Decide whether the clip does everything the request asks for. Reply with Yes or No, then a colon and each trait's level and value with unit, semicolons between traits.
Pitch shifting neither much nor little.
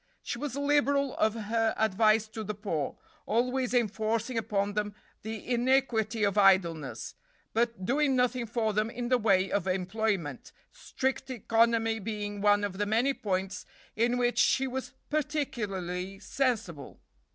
Yes: average, 3.5 semitones